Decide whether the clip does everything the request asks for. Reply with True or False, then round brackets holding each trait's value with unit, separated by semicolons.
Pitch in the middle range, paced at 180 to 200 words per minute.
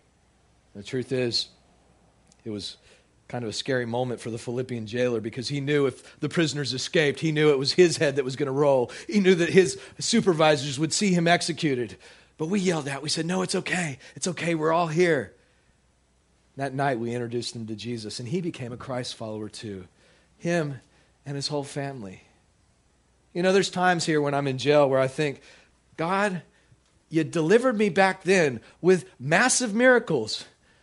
True (145 Hz; 185 wpm)